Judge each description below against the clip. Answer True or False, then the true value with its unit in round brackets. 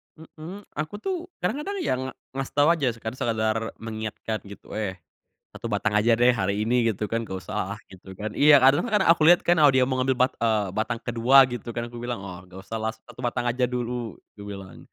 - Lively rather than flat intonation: False (3.8 semitones)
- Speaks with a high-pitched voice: False (120 Hz)